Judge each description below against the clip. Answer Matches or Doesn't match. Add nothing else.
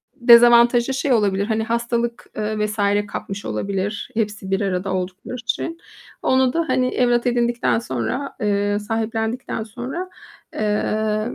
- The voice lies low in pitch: Doesn't match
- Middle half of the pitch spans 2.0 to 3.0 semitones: Matches